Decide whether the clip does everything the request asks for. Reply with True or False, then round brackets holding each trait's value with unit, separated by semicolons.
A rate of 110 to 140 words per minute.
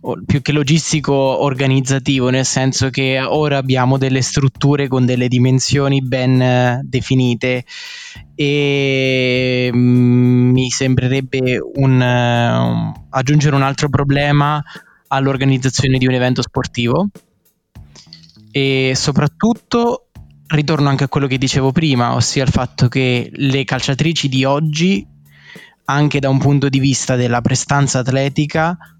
True (120 wpm)